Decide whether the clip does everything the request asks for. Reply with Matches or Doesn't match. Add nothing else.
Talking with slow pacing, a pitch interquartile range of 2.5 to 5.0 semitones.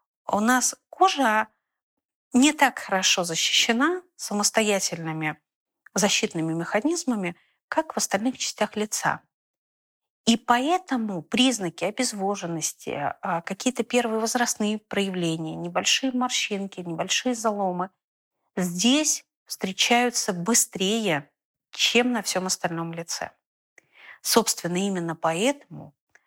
Doesn't match